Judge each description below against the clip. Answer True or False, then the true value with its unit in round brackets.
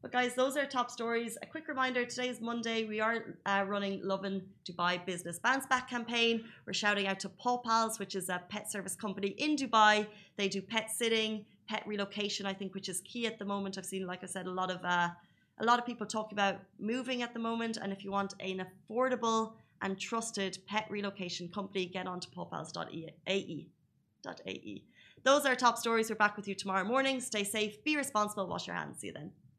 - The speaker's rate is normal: False (210 wpm)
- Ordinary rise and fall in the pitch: True (3.1 semitones)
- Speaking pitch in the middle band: False (210 Hz)